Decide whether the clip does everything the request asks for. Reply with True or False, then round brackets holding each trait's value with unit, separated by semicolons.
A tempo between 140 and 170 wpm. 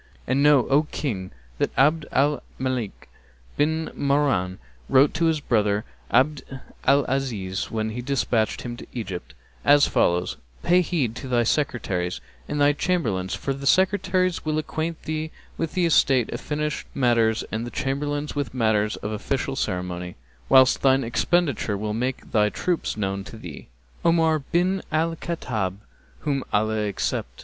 True (150 wpm)